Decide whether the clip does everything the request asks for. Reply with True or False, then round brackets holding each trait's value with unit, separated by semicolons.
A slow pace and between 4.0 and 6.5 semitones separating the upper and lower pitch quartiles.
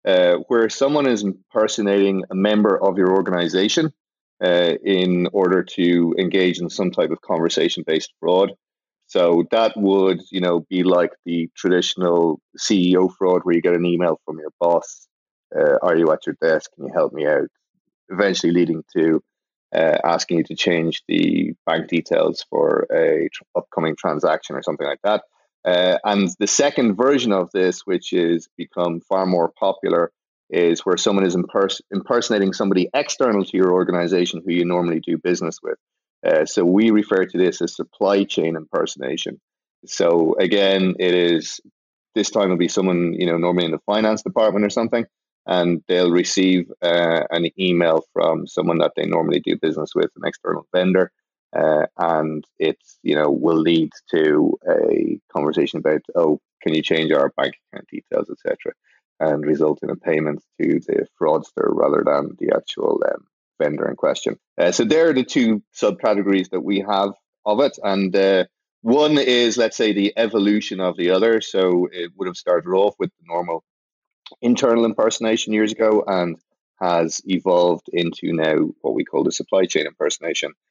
False (170 wpm; 4.5 semitones)